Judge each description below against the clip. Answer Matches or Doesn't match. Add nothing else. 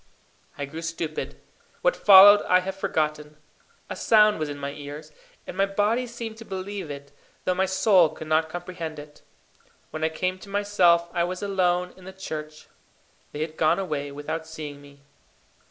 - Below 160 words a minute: Doesn't match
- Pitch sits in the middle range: Matches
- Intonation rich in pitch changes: Doesn't match